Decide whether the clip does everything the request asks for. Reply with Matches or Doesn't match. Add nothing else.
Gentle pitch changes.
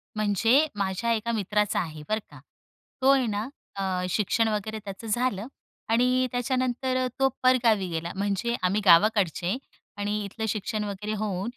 Doesn't match